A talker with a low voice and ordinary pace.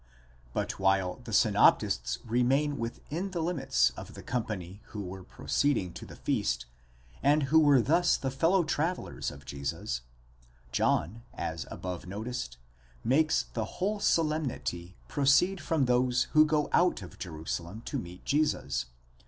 Yes: low, 125 Hz; average, 145 wpm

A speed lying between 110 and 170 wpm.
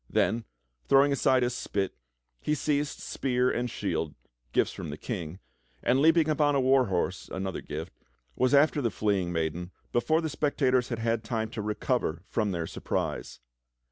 Yes: average, 165 wpm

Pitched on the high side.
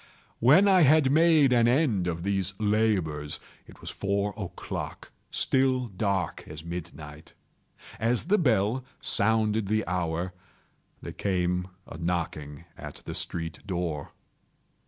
No: low, 100 Hz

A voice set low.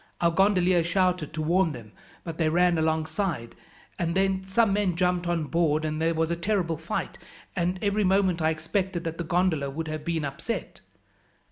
No: medium, 170 Hz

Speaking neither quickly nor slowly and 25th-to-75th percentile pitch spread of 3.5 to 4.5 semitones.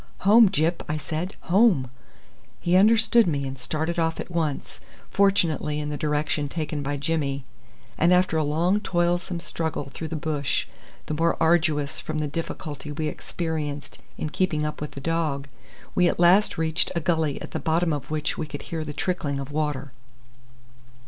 No: average, 175 wpm; average, 2.7 semitones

